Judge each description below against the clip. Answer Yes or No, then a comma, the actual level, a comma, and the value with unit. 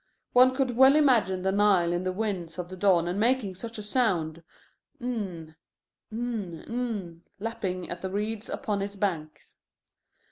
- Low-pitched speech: No, high, 200 Hz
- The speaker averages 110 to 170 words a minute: Yes, average, 150 wpm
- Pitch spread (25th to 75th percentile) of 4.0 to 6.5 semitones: Yes, average, 4.4 semitones